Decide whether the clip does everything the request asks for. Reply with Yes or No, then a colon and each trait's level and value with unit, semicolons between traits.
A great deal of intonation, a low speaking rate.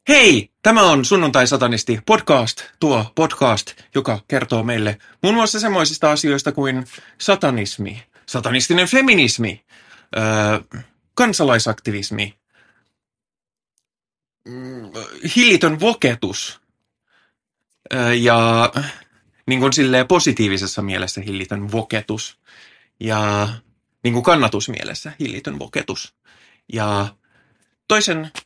Yes: wide, 5.7 semitones; slow, 80 wpm